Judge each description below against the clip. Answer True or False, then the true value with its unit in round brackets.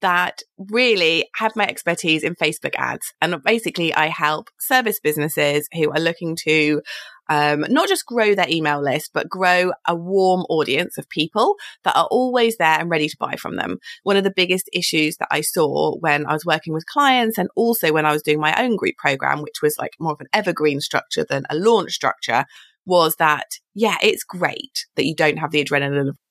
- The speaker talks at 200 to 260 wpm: True (205 wpm)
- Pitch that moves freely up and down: True (6.0 semitones)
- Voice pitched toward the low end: False (170 Hz)